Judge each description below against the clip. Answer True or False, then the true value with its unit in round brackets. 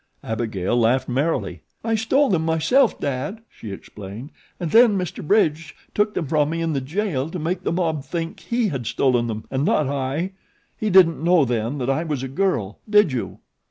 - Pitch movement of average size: False (6.0 semitones)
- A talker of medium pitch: True (155 Hz)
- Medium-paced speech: True (195 wpm)